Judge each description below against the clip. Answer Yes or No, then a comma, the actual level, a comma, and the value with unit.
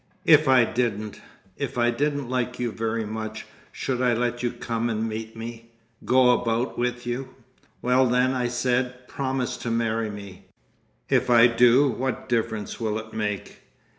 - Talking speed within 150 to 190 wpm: Yes, average, 155 wpm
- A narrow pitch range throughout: Yes, narrow, 1.8 semitones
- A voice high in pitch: No, low, 120 Hz